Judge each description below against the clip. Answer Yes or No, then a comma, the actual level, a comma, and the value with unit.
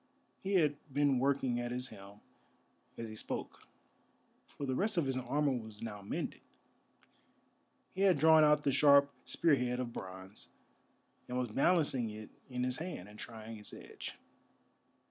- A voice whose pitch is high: No, low, 125 Hz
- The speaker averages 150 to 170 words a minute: Yes, average, 160 wpm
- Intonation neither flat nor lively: Yes, average, 4.7 semitones